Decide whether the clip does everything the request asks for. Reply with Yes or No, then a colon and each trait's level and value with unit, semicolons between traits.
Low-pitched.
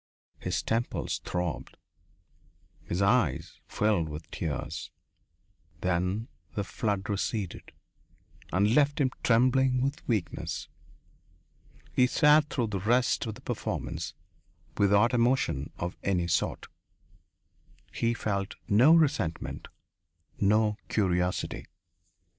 Yes: low, 105 Hz